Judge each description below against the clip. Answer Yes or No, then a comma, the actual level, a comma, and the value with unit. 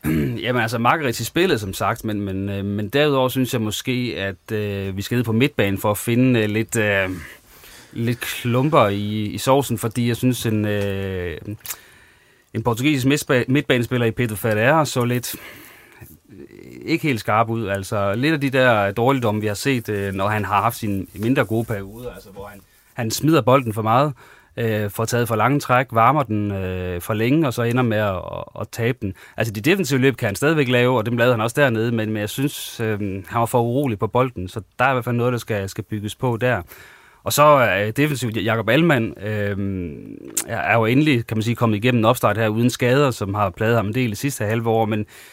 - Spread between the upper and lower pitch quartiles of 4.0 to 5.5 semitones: No, average, 3.2 semitones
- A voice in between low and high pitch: No, low, 115 Hz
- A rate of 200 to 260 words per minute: Yes, average, 210 wpm